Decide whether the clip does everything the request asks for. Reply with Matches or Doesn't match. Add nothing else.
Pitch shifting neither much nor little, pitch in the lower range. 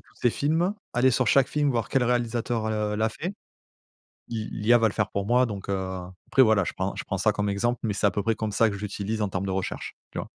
Matches